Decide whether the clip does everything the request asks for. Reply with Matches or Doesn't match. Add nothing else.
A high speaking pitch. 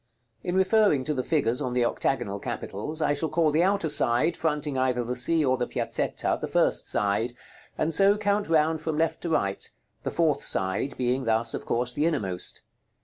Doesn't match